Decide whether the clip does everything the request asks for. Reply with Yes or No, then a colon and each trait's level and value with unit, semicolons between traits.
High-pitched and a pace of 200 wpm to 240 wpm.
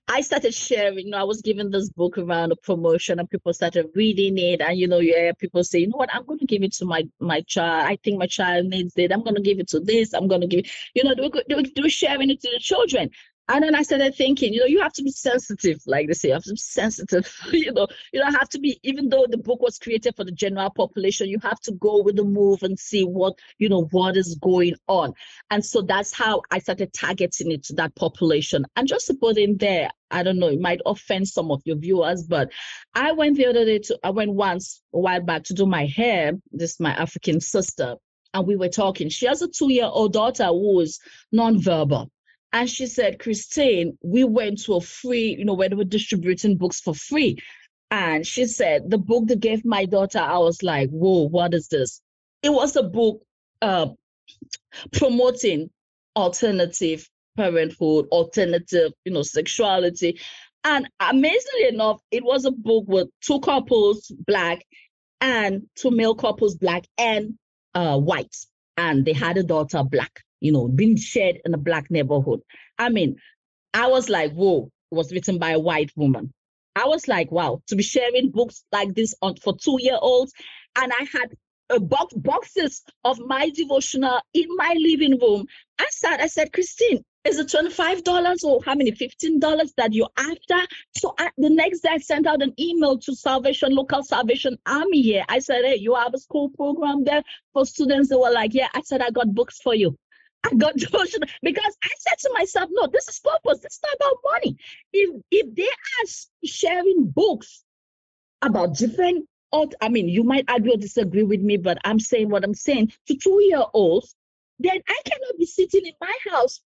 Yes: high, 220 Hz; fast, 205 wpm